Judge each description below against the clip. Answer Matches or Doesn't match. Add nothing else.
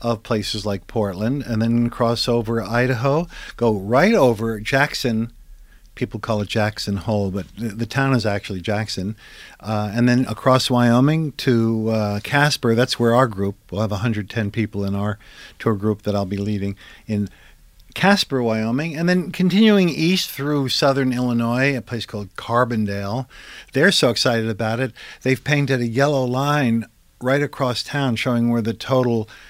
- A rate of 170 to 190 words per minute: Doesn't match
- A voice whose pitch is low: Matches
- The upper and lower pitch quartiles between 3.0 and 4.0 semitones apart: Matches